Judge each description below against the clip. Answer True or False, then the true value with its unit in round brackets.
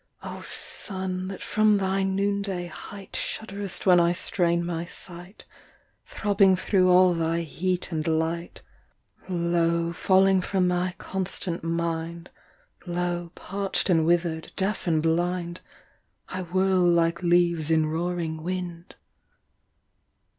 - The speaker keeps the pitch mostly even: True (1.9 semitones)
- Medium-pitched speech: True (175 Hz)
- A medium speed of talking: False (120 wpm)